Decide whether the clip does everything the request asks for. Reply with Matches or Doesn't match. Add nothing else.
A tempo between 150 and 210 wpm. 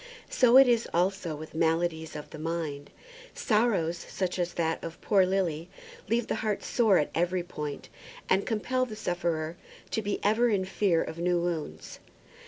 Matches